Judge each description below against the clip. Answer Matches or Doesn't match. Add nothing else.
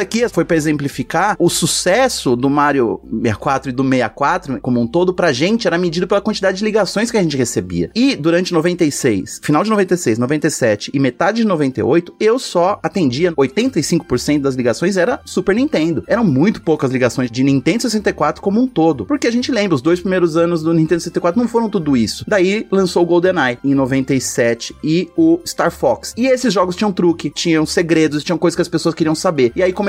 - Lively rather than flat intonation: Matches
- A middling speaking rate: Doesn't match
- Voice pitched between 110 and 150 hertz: Doesn't match